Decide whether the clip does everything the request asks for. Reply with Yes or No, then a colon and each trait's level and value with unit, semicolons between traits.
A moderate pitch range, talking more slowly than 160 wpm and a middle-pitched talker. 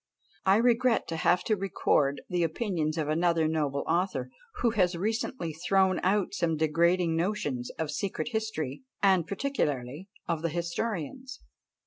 Yes: average, 4.3 semitones; average, 140 wpm; medium, 170 Hz